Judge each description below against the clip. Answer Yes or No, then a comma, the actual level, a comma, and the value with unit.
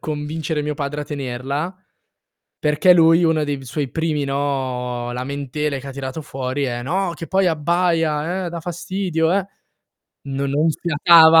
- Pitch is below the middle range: No, medium, 150 Hz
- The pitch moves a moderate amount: Yes, average, 3.1 semitones